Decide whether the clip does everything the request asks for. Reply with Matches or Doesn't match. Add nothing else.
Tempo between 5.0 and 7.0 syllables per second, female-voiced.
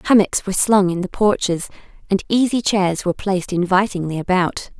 Matches